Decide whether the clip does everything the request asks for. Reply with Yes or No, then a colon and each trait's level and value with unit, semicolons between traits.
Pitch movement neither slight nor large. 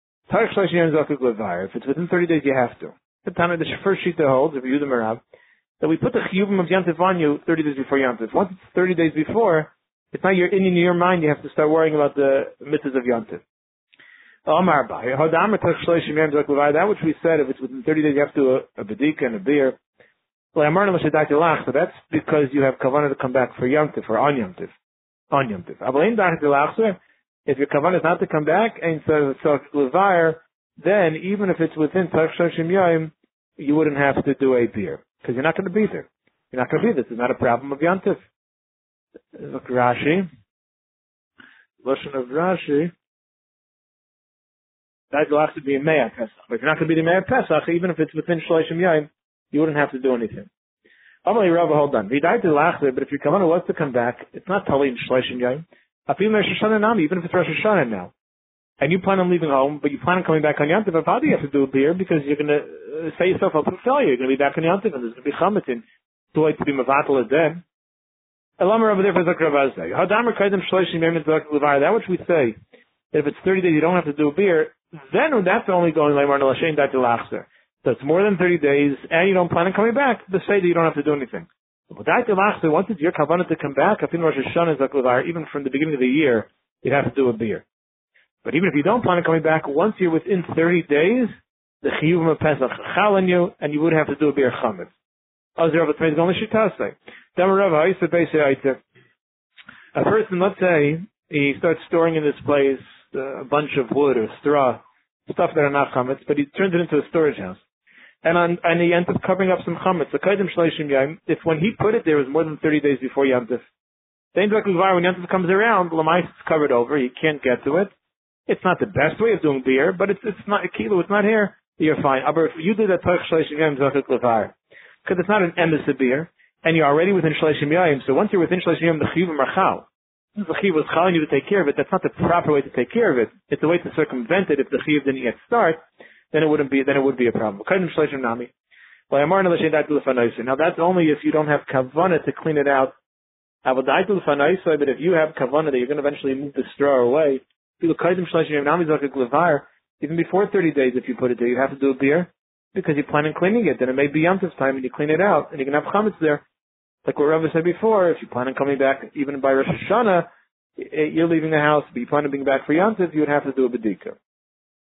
Yes: average, 4.2 semitones